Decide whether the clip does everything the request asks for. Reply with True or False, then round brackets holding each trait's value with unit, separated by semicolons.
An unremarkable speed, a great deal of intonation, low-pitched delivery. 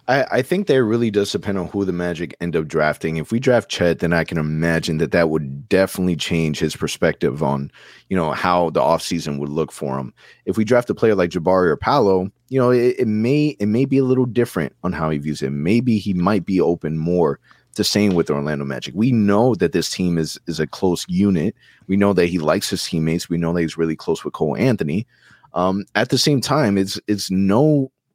False (230 wpm; 5.7 semitones; 95 Hz)